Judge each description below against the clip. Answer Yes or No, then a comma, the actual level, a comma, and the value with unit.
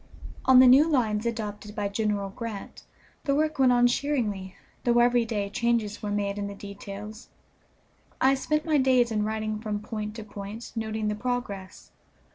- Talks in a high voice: Yes, high, 220 Hz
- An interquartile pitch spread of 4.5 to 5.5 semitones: No, average, 3.0 semitones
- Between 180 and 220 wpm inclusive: No, average, 170 wpm